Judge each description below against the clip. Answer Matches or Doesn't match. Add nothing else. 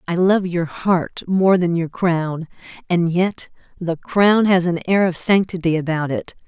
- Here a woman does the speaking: Matches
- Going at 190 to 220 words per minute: Doesn't match